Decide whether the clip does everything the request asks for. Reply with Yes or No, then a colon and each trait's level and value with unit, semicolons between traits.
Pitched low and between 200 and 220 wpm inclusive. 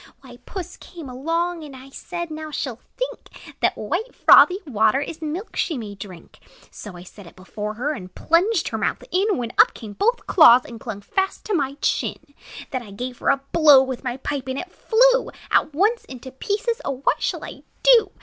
No: very high, 285 Hz; fast, 205 wpm